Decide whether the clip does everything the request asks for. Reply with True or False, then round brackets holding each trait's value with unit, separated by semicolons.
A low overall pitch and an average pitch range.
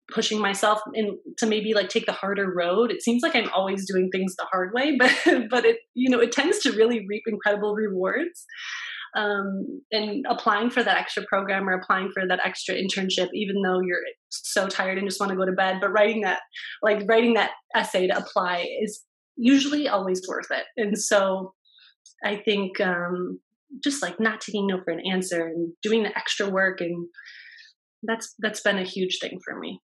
False (210 Hz; 3.4 semitones)